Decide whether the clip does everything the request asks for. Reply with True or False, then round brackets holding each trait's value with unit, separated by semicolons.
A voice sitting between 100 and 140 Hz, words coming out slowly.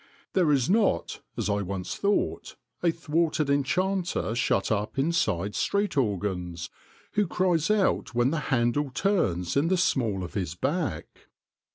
False (135 Hz; 145 wpm)